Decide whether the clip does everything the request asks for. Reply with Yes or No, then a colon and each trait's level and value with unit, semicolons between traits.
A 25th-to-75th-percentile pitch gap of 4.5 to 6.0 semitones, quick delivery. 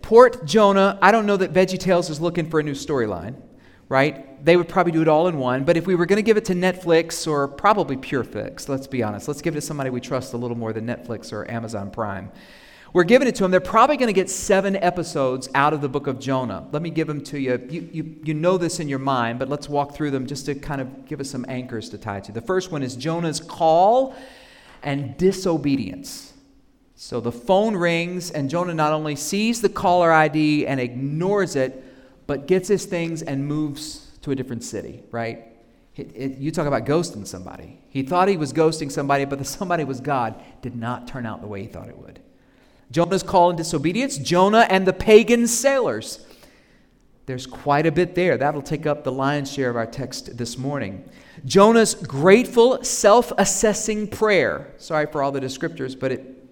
Yes: wide, 5.6 semitones; fast, 215 wpm